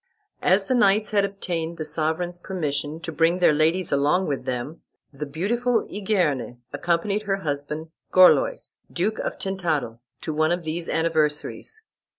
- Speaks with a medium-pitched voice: Yes, medium, 170 Hz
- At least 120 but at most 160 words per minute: Yes, average, 150 wpm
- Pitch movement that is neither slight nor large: Yes, average, 4.2 semitones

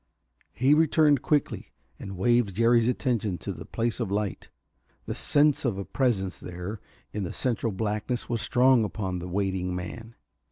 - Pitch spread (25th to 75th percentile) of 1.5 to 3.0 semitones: No, average, 4.3 semitones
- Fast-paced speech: No, average, 160 wpm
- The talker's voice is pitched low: Yes, low, 110 Hz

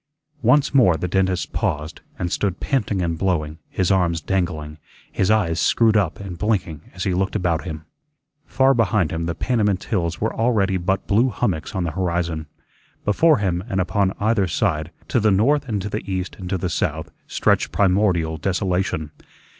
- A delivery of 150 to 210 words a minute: Yes, average, 180 wpm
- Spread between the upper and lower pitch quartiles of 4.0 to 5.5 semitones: No, average, 3.6 semitones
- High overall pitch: No, very low, 95 Hz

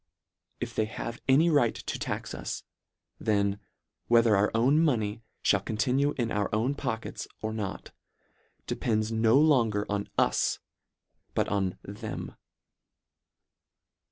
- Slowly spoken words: Yes, slow, 130 wpm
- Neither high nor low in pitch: No, low, 110 Hz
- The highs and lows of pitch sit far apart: No, average, 3.3 semitones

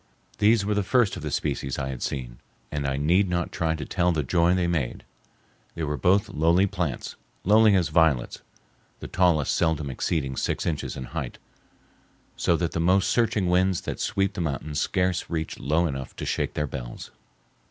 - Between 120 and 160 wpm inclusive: No, average, 180 wpm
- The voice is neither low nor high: No, very low, 85 Hz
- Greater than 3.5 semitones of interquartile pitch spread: Yes, average, 4.1 semitones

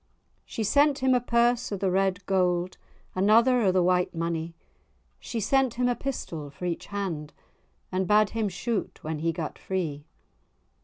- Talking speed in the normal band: Yes, average, 165 wpm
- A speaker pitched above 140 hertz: Yes, high, 190 Hz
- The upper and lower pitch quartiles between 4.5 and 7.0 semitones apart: Yes, average, 5.3 semitones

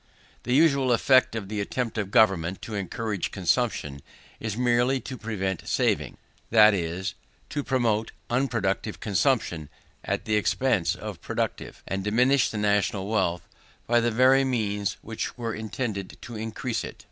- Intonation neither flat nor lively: Yes, average, 3.8 semitones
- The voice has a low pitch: Yes, low, 110 Hz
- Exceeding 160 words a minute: No, average, 145 wpm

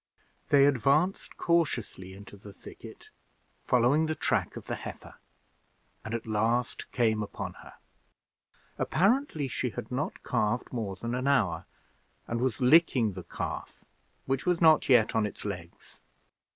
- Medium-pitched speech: No, low, 120 Hz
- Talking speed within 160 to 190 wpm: No, average, 140 wpm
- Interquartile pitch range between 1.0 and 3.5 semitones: No, average, 5.2 semitones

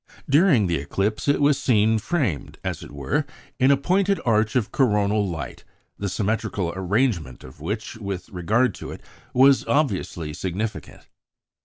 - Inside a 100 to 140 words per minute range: No, average, 150 wpm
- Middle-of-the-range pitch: No, low, 105 Hz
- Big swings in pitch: Yes, wide, 6.1 semitones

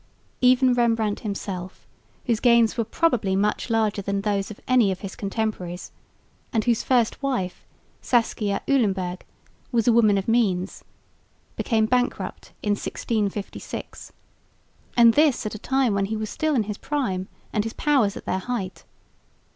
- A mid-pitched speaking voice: No, high, 220 Hz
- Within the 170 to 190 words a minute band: No, average, 150 wpm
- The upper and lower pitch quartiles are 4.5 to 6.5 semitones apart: No, average, 3.5 semitones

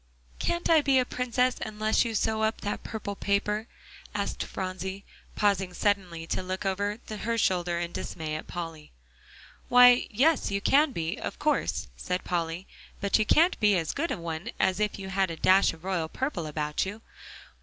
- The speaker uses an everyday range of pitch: Yes, average, 4.1 semitones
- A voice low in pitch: No, high, 200 Hz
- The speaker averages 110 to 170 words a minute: No, average, 180 wpm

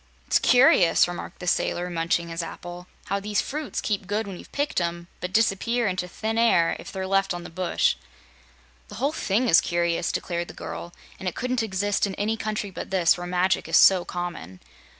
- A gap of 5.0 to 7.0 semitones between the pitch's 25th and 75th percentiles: No, average, 3.5 semitones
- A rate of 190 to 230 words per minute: Yes, average, 200 wpm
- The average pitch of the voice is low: No, high, 190 Hz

